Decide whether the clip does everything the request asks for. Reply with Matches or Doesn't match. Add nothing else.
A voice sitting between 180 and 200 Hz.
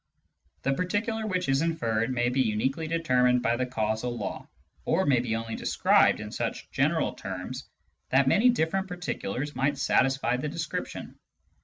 Doesn't match